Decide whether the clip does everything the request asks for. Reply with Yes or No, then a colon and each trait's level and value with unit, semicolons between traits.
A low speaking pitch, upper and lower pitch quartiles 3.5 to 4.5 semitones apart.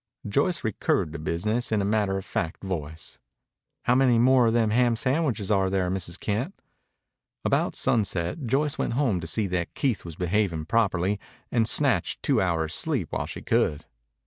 No: low, 105 Hz; wide, 5.4 semitones